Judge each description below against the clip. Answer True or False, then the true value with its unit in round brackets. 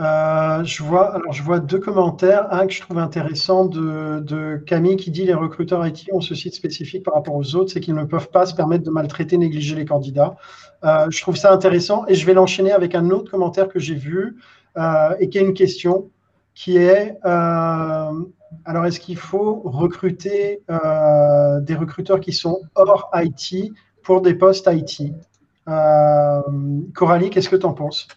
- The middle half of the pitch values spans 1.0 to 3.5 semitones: True (3.2 semitones)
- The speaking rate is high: False (190 wpm)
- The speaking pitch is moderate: True (175 Hz)